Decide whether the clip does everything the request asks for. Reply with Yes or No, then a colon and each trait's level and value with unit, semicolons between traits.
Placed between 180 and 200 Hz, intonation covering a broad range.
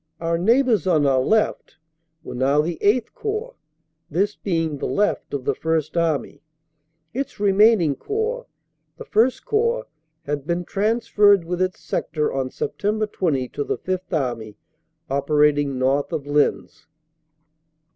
No: medium, 170 Hz; wide, 6.7 semitones